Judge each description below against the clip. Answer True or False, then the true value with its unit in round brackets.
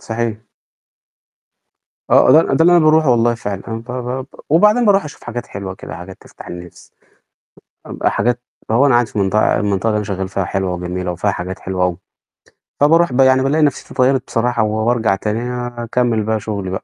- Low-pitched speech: True (115 Hz)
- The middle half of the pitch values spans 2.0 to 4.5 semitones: False (5.0 semitones)